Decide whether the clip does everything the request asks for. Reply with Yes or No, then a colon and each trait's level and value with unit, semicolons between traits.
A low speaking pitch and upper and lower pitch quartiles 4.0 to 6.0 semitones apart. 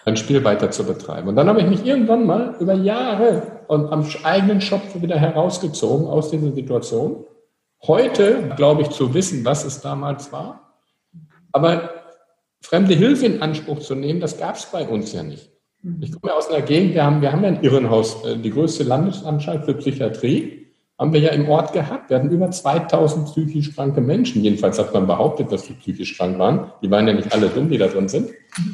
No: medium, 155 Hz; average, 4.4 semitones